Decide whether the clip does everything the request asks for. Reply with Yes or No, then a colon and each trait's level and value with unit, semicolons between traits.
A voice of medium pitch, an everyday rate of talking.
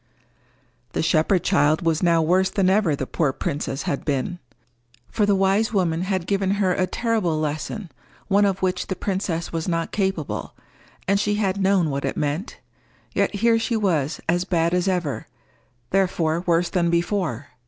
Yes: medium, 180 Hz; average, 170 wpm